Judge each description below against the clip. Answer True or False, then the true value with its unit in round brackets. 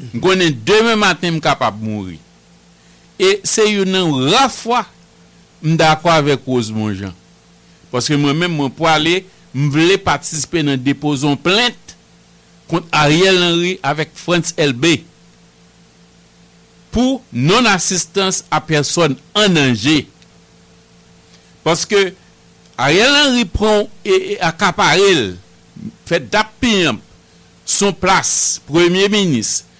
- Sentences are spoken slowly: True (110 wpm)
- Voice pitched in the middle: True (155 Hz)